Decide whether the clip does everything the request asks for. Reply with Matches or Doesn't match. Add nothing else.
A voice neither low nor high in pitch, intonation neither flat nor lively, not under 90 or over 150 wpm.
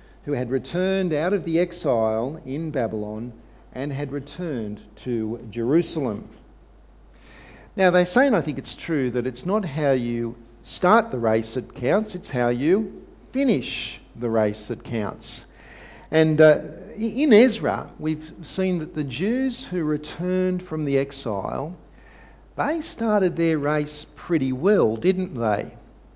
Doesn't match